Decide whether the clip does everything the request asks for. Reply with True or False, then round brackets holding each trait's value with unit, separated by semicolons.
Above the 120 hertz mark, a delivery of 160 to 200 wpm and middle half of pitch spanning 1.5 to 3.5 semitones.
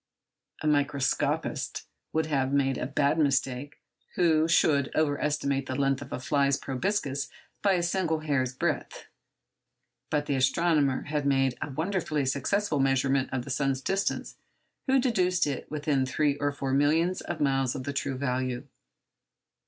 False (140 Hz; 150 wpm; 2.7 semitones)